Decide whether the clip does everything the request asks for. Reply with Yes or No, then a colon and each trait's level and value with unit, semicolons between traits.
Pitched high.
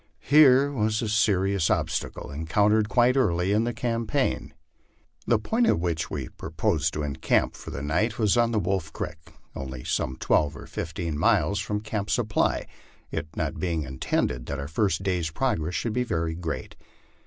No: very low, 95 Hz